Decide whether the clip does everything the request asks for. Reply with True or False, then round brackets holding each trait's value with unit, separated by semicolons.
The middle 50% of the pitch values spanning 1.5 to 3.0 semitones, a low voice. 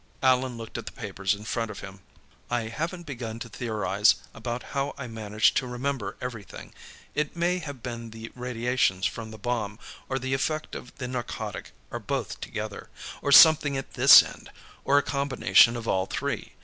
False (3.5 semitones; 120 Hz)